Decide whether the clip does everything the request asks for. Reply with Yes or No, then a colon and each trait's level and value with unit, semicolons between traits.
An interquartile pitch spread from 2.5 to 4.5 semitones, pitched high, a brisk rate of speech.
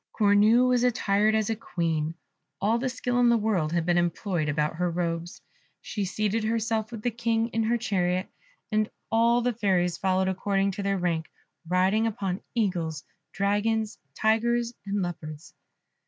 No: average, 4.2 semitones; high, 205 Hz; average, 160 wpm